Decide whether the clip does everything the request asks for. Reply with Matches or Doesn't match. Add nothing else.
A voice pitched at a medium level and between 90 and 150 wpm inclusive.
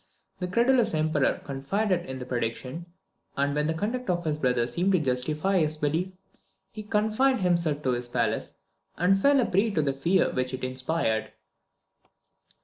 Doesn't match